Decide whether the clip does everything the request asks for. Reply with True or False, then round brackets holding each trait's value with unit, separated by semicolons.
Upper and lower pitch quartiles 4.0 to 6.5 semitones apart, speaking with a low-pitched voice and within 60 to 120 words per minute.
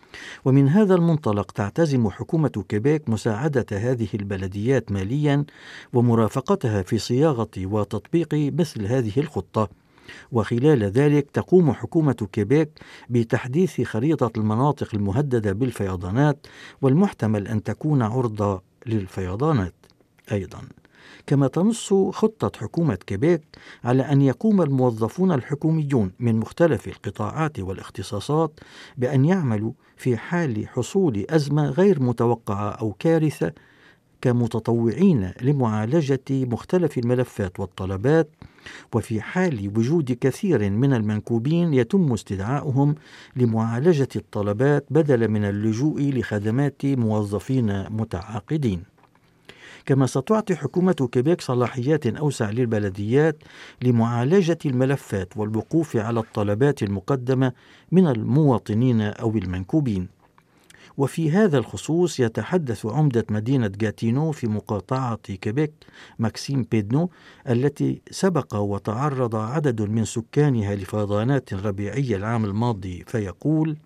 True (5.4 semitones; 125 Hz; 95 wpm)